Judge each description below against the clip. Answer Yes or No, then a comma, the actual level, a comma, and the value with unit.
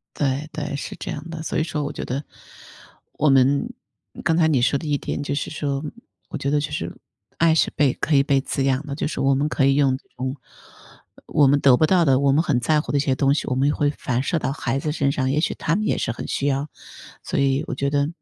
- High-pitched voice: No, medium, 140 Hz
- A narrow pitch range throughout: Yes, narrow, 1.9 semitones